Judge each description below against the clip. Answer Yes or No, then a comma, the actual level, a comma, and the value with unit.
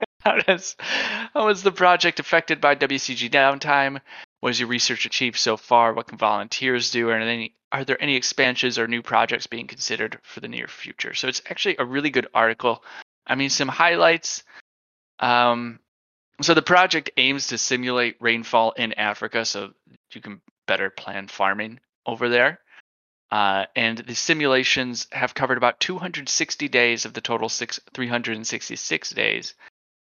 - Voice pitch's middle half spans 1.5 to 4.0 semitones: Yes, average, 3.3 semitones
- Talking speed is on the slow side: No, average, 160 wpm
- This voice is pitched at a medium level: No, low, 120 Hz